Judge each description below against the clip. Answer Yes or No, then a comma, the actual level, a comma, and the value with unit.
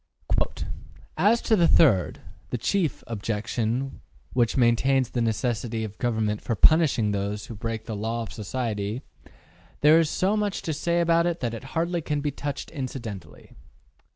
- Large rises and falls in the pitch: Yes, wide, 6.2 semitones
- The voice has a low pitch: Yes, low, 125 Hz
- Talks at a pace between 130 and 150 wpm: No, average, 160 wpm